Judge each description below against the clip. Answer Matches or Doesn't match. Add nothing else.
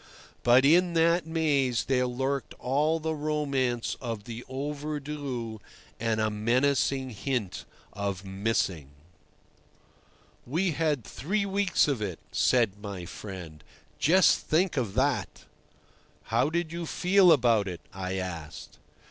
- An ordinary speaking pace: Doesn't match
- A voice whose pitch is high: Doesn't match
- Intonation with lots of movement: Matches